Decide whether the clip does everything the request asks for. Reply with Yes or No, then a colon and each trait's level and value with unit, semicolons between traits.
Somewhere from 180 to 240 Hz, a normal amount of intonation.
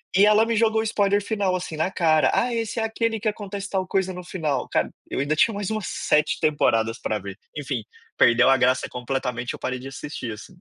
No: medium, 185 Hz; wide, 7.8 semitones